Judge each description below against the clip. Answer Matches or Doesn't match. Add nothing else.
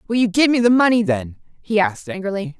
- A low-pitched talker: Doesn't match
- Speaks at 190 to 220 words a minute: Doesn't match